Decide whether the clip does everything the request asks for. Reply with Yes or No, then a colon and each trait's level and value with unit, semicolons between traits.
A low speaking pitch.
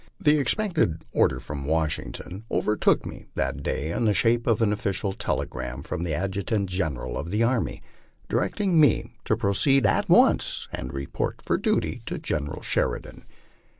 Yes: low, 100 Hz